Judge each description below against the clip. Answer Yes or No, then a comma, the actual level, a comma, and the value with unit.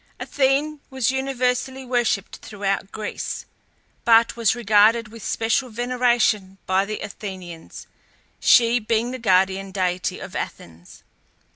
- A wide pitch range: No, average, 4.2 semitones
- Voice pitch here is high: Yes, high, 225 Hz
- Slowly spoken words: Yes, slow, 115 wpm